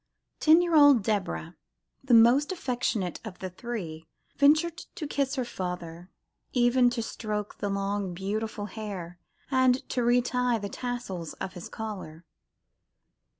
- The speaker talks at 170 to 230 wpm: No, average, 140 wpm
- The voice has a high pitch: Yes, high, 220 Hz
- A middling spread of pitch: Yes, average, 4.9 semitones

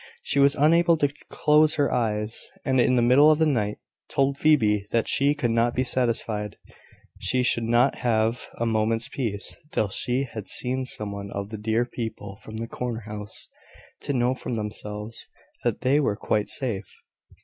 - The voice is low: Yes, low, 120 Hz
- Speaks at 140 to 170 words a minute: No, average, 180 wpm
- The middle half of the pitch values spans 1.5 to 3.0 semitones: No, average, 3.9 semitones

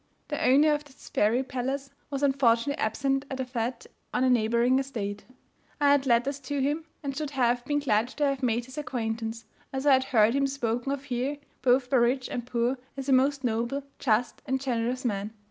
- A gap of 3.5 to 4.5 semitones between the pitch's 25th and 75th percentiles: No, average, 2.7 semitones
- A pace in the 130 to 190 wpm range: No, average, 200 wpm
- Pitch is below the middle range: No, very high, 260 Hz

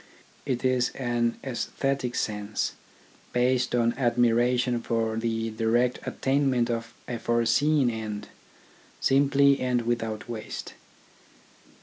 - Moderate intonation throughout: No, narrow, 1.9 semitones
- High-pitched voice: No, low, 120 Hz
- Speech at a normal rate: No, slow, 100 wpm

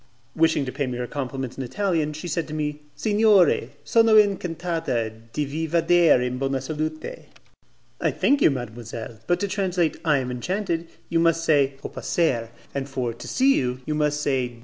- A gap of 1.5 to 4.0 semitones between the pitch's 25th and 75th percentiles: No, average, 4.9 semitones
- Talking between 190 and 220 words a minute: Yes, average, 195 wpm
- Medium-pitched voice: Yes, medium, 150 Hz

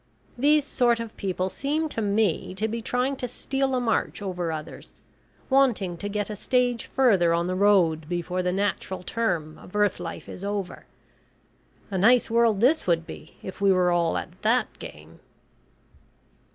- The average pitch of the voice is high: Yes, high, 205 Hz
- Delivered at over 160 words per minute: Yes, average, 170 wpm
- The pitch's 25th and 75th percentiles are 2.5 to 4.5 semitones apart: No, average, 5.0 semitones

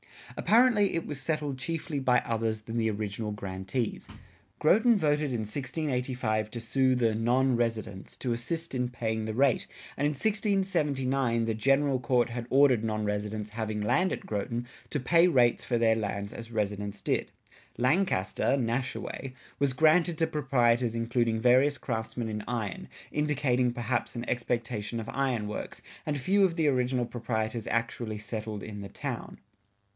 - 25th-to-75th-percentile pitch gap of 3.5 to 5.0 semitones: Yes, average, 4.0 semitones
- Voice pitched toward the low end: Yes, low, 120 Hz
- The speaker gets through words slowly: No, average, 155 wpm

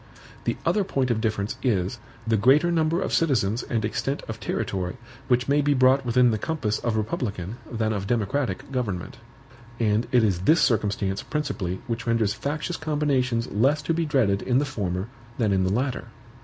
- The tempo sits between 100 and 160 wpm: No, average, 180 wpm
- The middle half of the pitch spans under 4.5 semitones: No, average, 5.0 semitones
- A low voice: Yes, low, 120 Hz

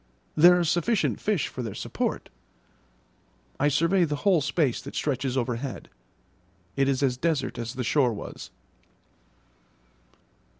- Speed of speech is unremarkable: No, slow, 130 wpm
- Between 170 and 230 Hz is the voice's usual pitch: No, medium, 145 Hz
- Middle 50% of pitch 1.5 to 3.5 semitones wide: No, average, 4.8 semitones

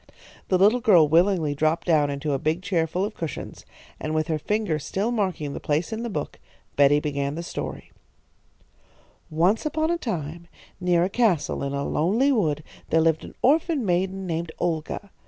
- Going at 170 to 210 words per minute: Yes, average, 180 wpm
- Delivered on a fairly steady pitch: No, average, 4.9 semitones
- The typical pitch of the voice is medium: Yes, medium, 170 Hz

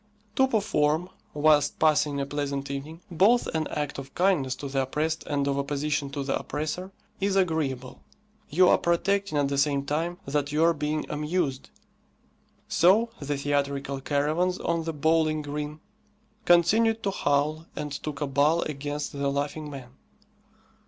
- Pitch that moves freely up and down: No, average, 2.8 semitones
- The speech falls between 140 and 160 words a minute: Yes, average, 150 wpm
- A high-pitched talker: No, medium, 150 Hz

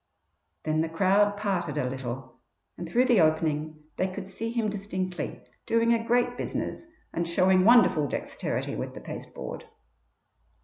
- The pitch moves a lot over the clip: Yes, wide, 5.9 semitones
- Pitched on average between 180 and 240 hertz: Yes, medium, 185 Hz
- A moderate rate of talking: Yes, average, 145 wpm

